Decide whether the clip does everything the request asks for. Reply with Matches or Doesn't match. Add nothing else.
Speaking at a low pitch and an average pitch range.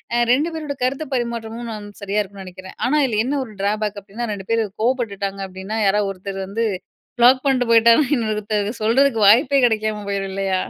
Doesn't match